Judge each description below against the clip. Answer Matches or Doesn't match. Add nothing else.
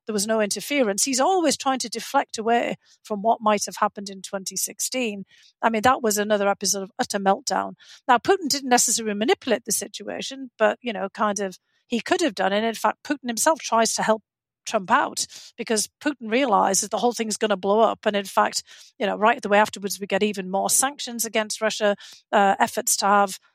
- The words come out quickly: Matches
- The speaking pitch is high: Matches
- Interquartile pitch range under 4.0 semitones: Matches